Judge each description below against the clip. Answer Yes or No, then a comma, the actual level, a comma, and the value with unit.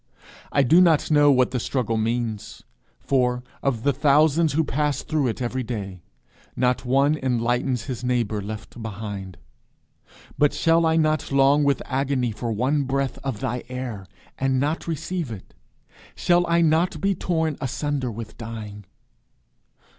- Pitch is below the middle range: Yes, low, 130 Hz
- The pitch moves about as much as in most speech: Yes, average, 4.1 semitones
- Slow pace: No, average, 150 wpm